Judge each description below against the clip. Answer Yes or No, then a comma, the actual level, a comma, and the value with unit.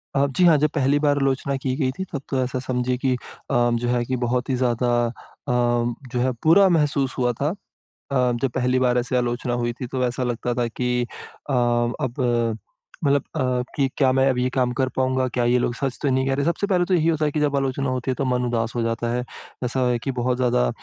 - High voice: No, low, 130 Hz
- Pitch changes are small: Yes, narrow, 2.0 semitones